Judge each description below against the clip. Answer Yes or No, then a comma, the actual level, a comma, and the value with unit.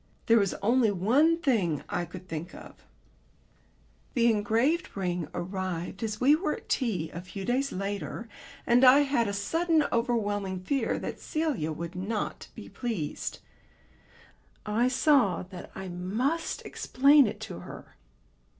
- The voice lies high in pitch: Yes, high, 215 Hz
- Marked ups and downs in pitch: Yes, wide, 6.0 semitones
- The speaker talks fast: No, average, 140 wpm